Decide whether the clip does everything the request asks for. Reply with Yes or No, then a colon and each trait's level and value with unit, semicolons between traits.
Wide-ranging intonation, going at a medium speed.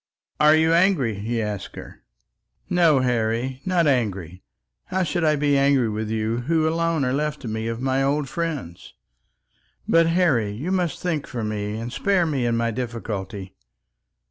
Yes: wide, 6.2 semitones; average, 170 wpm